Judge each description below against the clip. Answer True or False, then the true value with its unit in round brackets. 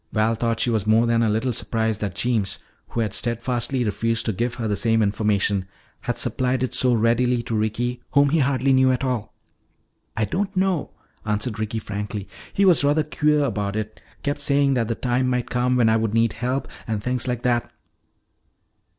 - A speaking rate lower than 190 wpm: False (195 wpm)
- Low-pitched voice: True (115 Hz)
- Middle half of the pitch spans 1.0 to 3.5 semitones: True (2.8 semitones)